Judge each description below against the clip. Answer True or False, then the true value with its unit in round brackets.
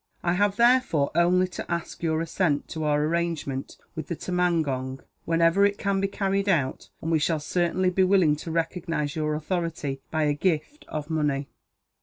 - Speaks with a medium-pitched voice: True (165 Hz)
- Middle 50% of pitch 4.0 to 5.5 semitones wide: False (3.3 semitones)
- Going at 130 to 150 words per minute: False (175 wpm)